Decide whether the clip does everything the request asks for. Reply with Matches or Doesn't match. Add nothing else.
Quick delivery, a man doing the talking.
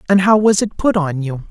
Matches